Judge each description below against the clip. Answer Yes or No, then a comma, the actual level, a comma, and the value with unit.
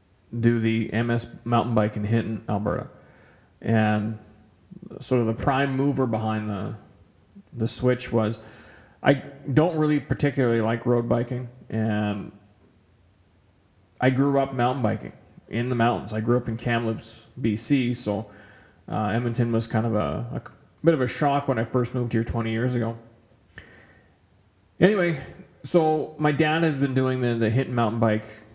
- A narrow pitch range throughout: No, average, 3.2 semitones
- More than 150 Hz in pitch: No, low, 115 Hz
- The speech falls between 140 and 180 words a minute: Yes, average, 155 wpm